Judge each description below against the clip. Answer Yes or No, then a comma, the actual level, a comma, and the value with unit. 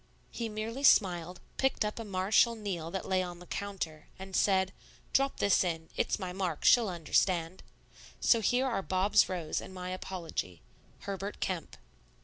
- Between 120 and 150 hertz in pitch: No, high, 190 Hz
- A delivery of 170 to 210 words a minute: No, average, 160 wpm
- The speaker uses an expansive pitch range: No, average, 3.0 semitones